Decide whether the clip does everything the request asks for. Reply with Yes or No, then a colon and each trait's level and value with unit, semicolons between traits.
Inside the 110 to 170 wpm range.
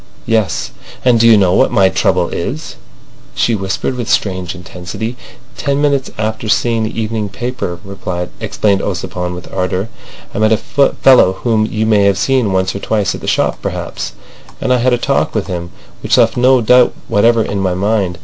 No: average, 185 wpm